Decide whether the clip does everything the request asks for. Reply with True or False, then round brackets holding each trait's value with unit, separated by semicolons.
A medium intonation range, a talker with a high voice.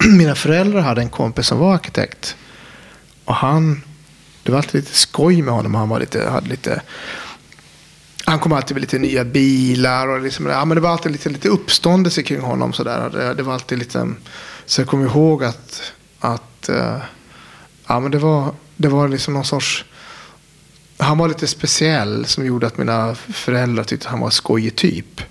False (3.8 semitones; 140 Hz)